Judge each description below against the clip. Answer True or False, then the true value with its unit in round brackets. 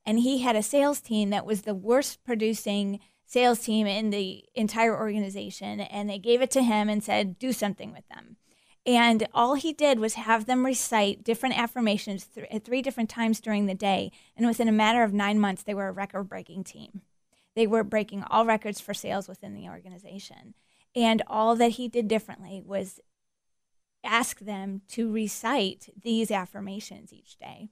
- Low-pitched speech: False (215 Hz)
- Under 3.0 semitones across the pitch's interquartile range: True (2.6 semitones)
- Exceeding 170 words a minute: True (185 wpm)